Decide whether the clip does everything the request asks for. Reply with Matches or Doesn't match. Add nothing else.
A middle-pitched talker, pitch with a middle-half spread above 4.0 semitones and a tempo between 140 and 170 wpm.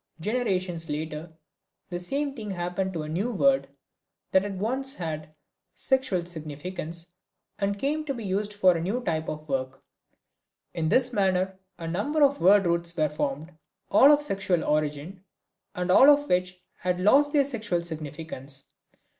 Matches